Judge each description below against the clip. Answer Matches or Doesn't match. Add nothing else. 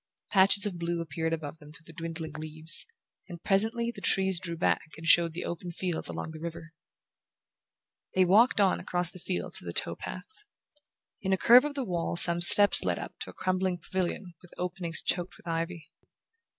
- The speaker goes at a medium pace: Matches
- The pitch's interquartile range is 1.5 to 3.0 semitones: Matches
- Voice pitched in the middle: Matches